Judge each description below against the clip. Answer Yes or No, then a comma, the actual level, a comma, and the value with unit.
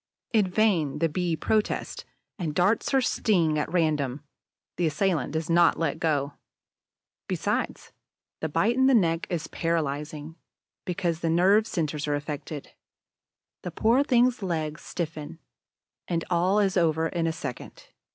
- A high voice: No, medium, 165 Hz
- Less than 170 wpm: Yes, average, 140 wpm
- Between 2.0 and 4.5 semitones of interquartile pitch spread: Yes, average, 3.6 semitones